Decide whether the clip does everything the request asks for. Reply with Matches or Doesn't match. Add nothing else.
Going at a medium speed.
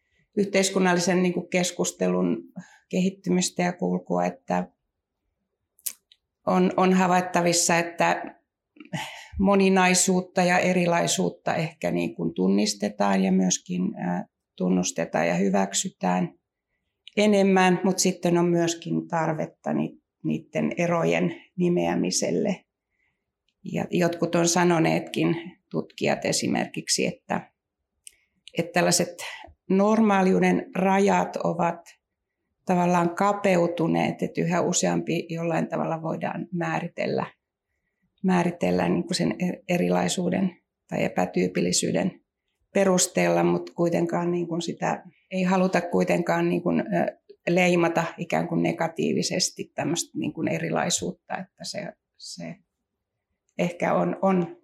Doesn't match